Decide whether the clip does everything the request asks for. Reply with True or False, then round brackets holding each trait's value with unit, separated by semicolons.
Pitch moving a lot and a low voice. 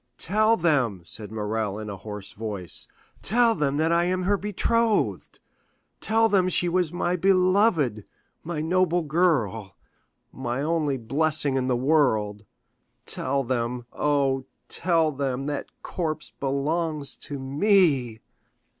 False (6.5 semitones; 150 Hz)